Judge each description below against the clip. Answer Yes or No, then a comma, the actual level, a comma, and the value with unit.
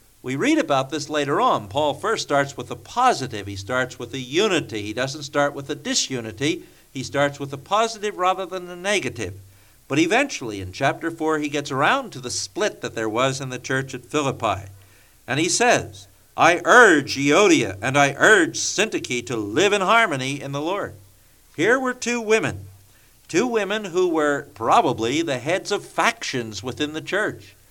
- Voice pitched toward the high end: No, medium, 140 Hz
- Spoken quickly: No, average, 180 wpm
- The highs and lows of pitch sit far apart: Yes, wide, 5.9 semitones